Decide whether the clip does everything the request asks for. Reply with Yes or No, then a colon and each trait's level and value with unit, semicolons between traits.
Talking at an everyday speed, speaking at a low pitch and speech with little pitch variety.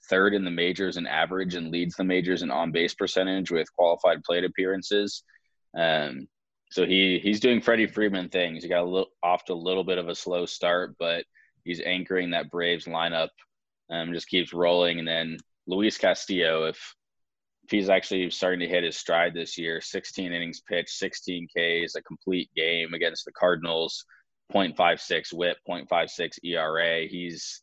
Yes: average, 175 wpm; very low, 85 Hz; narrow, 1.8 semitones